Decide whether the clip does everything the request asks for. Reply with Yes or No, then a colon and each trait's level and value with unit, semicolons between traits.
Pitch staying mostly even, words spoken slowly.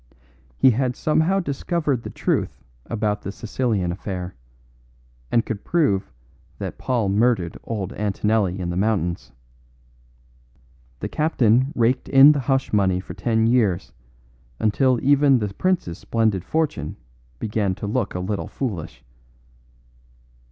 No: average, 5.2 semitones; slow, 130 wpm